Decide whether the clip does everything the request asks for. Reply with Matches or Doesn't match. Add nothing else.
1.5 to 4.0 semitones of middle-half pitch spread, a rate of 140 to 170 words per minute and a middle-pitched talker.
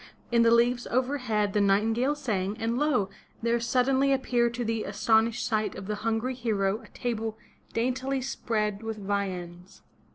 Doesn't match